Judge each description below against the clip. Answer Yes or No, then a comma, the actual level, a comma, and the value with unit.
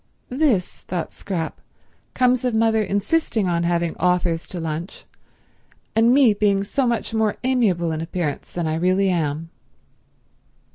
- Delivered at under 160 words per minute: Yes, average, 140 wpm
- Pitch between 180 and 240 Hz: Yes, high, 190 Hz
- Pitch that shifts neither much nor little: Yes, average, 4.9 semitones